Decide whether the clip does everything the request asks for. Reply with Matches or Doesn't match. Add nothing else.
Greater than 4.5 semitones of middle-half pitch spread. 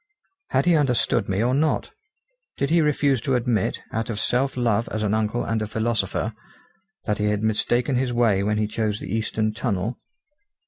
Doesn't match